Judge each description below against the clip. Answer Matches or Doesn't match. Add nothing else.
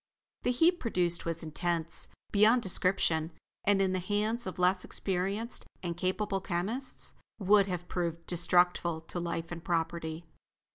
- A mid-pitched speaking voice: Matches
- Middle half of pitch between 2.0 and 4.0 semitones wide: Matches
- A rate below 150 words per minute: Matches